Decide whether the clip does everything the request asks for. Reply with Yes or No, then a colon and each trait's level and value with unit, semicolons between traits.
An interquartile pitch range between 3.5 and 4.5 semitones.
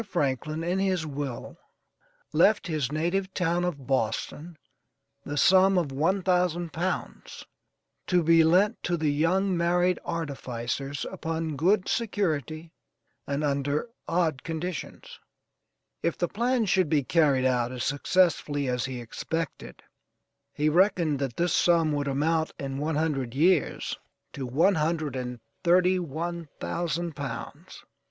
Yes: average, 3.9 semitones